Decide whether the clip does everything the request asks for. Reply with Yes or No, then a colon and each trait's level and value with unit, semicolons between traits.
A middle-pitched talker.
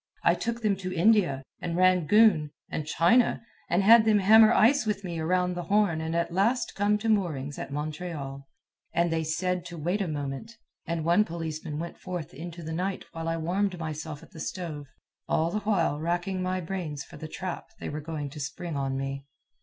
Yes: medium, 170 Hz